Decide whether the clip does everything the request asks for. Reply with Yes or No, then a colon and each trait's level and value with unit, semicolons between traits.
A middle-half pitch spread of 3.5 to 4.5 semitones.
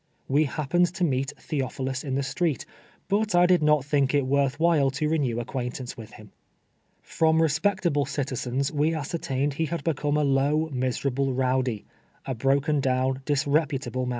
No: average, 2.8 semitones